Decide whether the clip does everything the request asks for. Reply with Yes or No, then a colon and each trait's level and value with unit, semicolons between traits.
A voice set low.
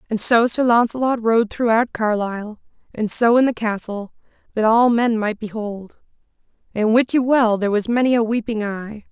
No: high, 225 Hz